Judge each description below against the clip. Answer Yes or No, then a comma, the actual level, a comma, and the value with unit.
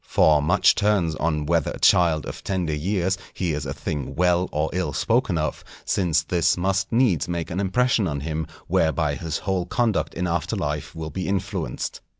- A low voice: Yes, very low, 85 Hz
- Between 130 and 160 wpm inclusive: No, average, 180 wpm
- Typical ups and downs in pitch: Yes, average, 3.6 semitones